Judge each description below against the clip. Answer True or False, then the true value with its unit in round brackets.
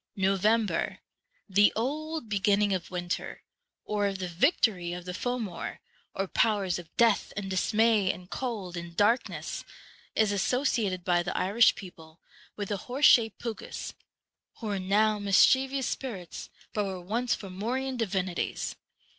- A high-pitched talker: True (205 Hz)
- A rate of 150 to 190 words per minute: False (140 wpm)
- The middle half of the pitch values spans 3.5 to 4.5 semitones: True (3.8 semitones)